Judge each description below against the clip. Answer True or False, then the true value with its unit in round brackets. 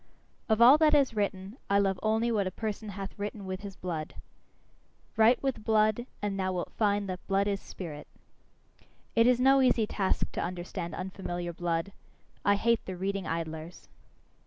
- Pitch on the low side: False (200 Hz)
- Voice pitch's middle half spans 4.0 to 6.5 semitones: False (3.1 semitones)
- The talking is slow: False (170 wpm)